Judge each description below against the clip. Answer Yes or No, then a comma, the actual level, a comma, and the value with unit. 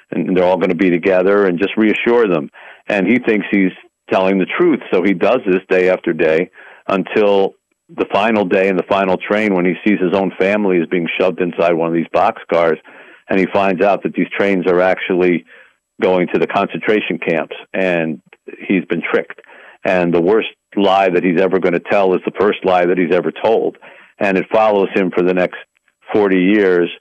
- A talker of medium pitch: No, very low, 90 Hz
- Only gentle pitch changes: Yes, narrow, 1.8 semitones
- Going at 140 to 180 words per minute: No, fast, 205 wpm